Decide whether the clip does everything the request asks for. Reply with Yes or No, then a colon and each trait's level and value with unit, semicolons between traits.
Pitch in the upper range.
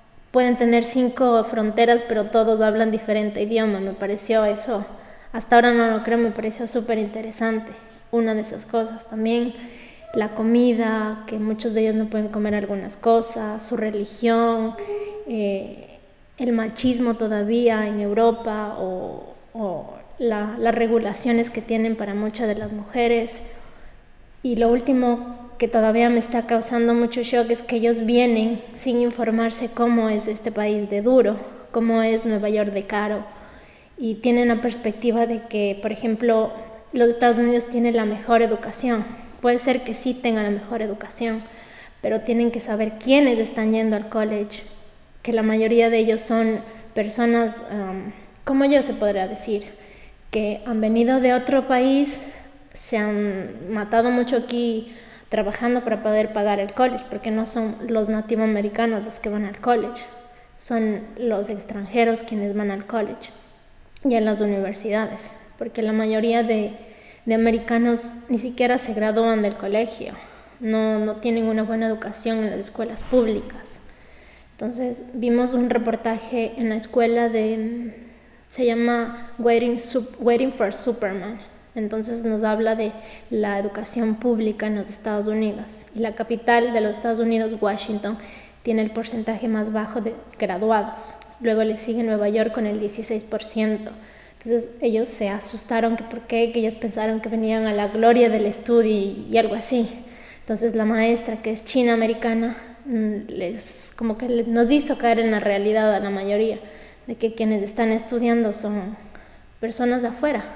Yes: high, 225 Hz